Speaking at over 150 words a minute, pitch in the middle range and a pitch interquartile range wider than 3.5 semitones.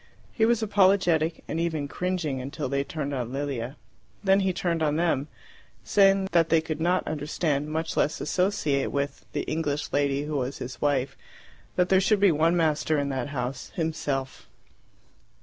Yes: average, 165 wpm; medium, 155 Hz; average, 3.9 semitones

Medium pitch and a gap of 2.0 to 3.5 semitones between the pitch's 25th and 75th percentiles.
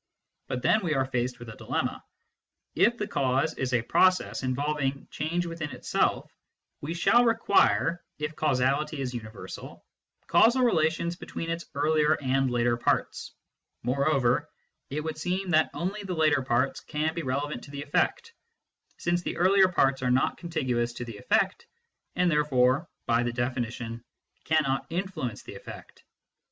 No: medium, 145 Hz; average, 4.9 semitones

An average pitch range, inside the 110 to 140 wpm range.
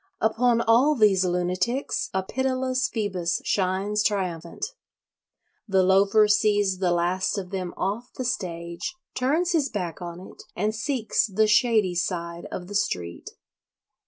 Yes: average, 4.2 semitones; slow, 135 wpm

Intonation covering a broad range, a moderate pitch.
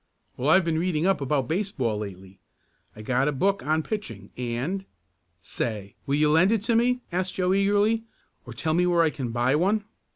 Yes: wide, 8.0 semitones; medium, 155 Hz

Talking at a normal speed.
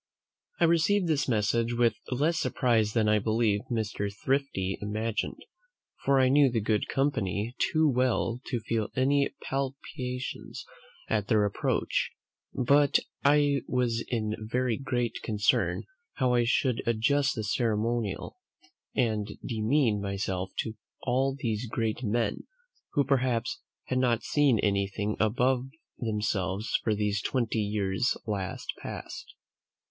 No: slow, 125 wpm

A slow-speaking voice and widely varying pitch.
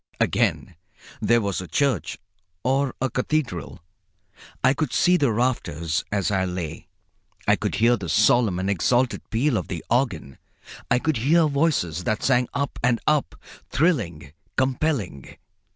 No: average, 145 wpm; wide, 7.0 semitones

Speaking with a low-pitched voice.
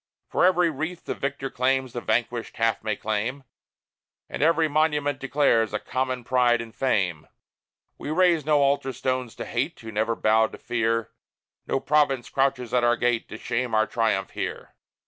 Yes: low, 125 Hz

